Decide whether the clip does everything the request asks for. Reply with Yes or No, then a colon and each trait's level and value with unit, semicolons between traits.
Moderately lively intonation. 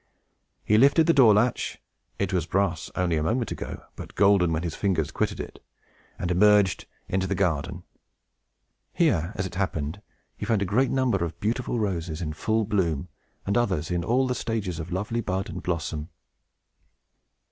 Yes: average, 4.5 semitones